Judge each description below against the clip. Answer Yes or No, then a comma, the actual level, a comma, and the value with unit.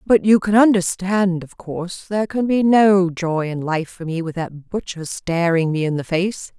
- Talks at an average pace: No, fast, 210 wpm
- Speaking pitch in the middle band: Yes, medium, 180 Hz